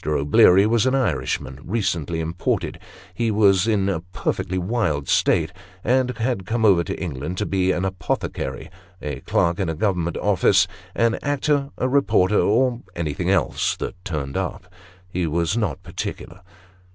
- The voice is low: Yes, very low, 95 Hz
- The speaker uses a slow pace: No, average, 150 wpm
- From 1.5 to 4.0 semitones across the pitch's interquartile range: No, average, 4.8 semitones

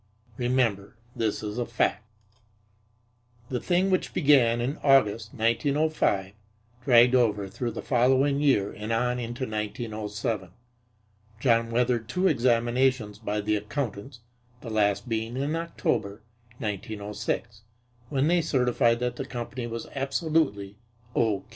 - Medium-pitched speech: No, low, 120 Hz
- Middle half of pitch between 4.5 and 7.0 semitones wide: No, average, 3.7 semitones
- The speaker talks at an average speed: No, slow, 125 wpm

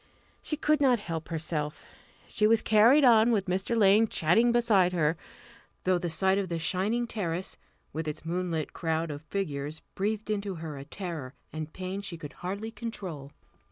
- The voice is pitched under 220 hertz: Yes, medium, 185 Hz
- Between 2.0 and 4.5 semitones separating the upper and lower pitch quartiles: No, average, 5.1 semitones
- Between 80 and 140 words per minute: No, average, 170 wpm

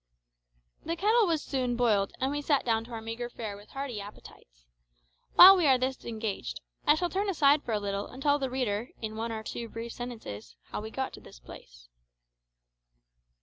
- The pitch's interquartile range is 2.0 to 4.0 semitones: No, average, 4.8 semitones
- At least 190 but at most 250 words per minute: Yes, average, 195 wpm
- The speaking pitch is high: Yes, high, 240 Hz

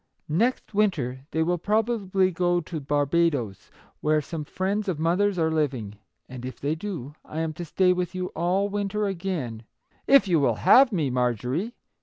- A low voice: No, medium, 170 Hz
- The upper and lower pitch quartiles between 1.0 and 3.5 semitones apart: No, average, 5.0 semitones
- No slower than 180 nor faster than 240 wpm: Yes, average, 185 wpm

